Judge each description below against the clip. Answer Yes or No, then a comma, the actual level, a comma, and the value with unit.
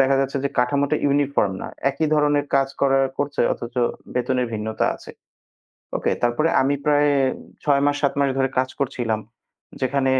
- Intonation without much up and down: Yes, narrow, 1.9 semitones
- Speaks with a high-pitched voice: No, low, 135 Hz